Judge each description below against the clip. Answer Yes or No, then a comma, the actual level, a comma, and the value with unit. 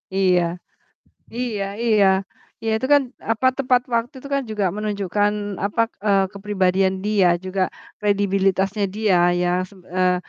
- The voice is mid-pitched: No, high, 205 Hz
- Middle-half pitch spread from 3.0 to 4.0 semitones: No, narrow, 2.4 semitones